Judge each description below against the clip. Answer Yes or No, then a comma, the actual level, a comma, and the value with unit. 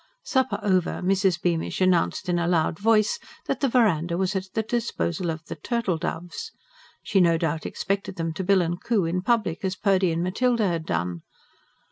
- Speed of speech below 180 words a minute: No, average, 185 wpm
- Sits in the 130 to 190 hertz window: Yes, medium, 185 Hz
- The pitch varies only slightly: No, average, 3.2 semitones